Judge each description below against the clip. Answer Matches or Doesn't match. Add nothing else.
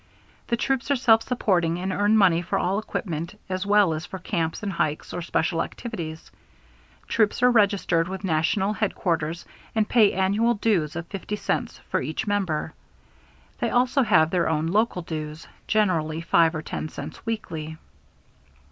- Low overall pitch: Doesn't match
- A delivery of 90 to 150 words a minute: Doesn't match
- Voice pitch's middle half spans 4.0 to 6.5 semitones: Matches